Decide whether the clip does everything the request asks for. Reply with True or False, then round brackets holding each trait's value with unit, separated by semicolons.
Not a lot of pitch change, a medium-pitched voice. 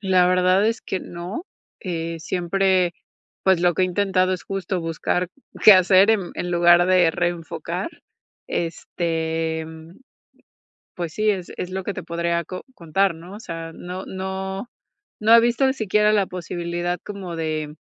True (2.1 semitones; 180 Hz)